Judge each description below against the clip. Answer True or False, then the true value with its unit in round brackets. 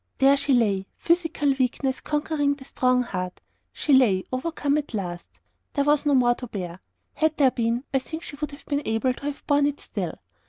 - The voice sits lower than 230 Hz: False (270 Hz)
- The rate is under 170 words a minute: False (200 wpm)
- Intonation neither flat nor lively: True (3.3 semitones)